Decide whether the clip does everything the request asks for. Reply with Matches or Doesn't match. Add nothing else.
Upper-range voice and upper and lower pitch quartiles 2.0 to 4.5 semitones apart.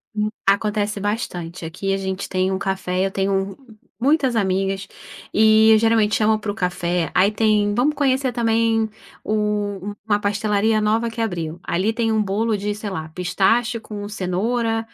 Matches